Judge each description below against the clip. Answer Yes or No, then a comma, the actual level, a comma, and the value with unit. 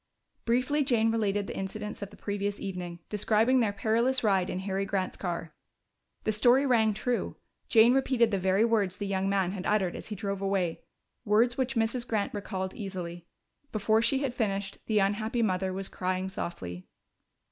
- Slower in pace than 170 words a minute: No, average, 175 wpm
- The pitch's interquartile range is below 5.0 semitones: Yes, average, 3.1 semitones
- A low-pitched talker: No, high, 205 Hz